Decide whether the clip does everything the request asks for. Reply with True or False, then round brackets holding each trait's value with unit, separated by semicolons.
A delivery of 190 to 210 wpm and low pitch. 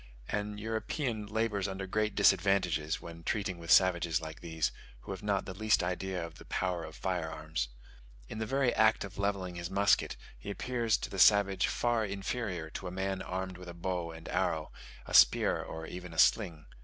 True (195 wpm; 95 Hz)